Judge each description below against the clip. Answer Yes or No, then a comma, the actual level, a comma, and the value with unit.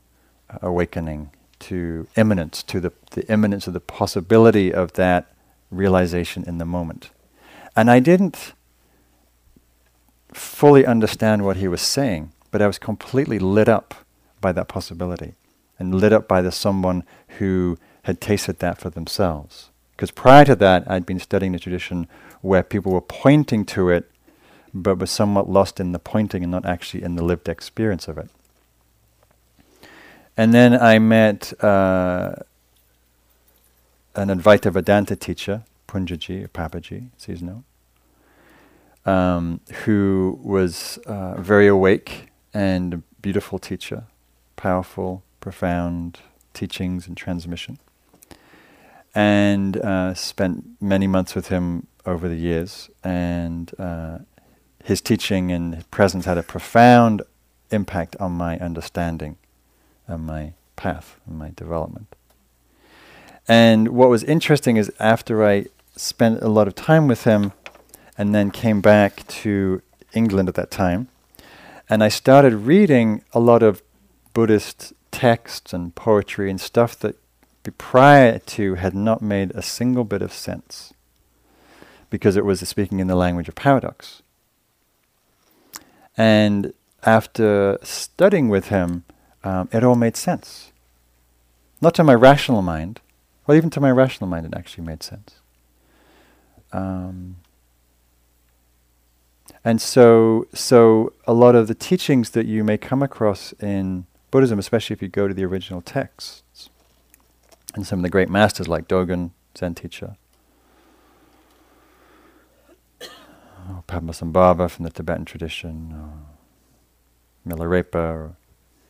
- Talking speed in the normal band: No, slow, 130 wpm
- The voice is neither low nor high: No, very low, 95 Hz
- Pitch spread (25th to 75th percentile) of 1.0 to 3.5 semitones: No, average, 4.2 semitones